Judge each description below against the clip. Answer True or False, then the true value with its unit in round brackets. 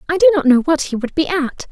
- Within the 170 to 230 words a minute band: False (315 wpm)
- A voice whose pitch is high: True (310 Hz)